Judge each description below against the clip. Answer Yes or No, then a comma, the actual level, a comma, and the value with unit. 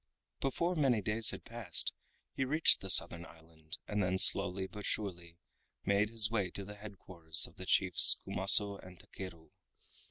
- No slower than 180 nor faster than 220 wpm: No, average, 165 wpm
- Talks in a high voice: No, low, 100 Hz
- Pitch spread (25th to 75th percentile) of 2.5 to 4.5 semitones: Yes, average, 3.6 semitones